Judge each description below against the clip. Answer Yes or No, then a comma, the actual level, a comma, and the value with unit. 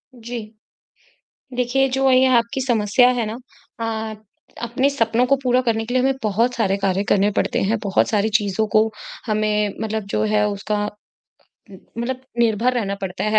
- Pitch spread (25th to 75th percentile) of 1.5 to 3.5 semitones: Yes, average, 2.9 semitones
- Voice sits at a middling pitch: No, high, 225 Hz